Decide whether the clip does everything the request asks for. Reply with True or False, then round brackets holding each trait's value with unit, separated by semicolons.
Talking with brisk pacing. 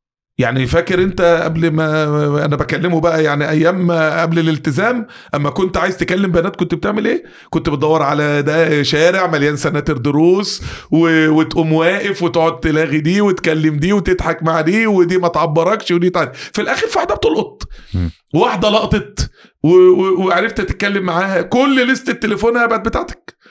True (150 wpm)